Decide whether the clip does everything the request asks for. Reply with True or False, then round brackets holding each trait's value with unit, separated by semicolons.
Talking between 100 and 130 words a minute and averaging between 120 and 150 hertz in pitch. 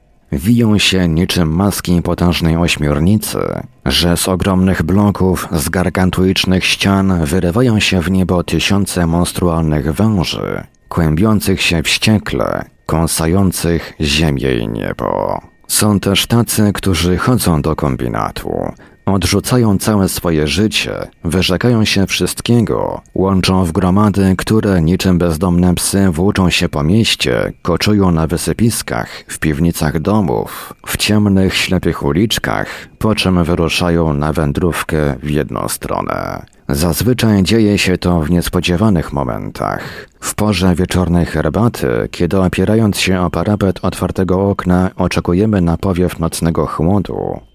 False (120 wpm; 90 Hz)